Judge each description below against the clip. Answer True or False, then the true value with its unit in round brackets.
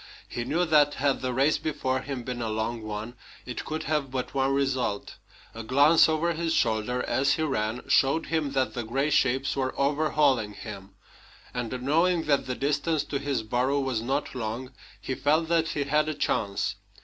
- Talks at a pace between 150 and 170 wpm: False (185 wpm)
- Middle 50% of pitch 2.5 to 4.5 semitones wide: True (3.6 semitones)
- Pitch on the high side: False (135 Hz)